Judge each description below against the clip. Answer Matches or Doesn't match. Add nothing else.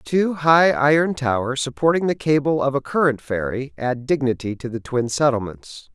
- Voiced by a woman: Doesn't match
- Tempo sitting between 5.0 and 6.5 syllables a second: Doesn't match